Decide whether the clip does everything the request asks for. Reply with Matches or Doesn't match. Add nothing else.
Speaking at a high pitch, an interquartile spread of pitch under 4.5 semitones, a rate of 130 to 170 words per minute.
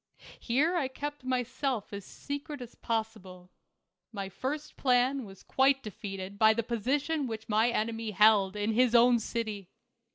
Matches